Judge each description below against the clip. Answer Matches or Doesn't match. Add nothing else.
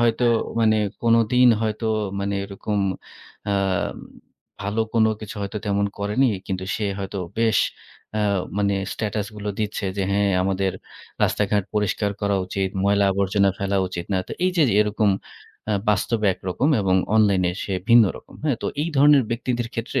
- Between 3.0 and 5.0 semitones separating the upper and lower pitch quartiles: Doesn't match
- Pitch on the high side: Doesn't match